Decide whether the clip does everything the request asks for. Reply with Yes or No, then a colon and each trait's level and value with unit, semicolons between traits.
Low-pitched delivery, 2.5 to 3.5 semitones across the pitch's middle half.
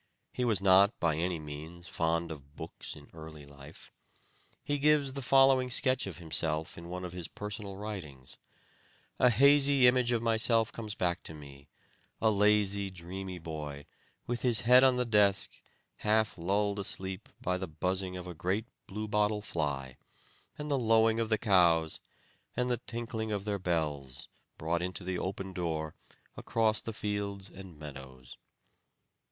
No: very low, 95 Hz; average, 5.2 semitones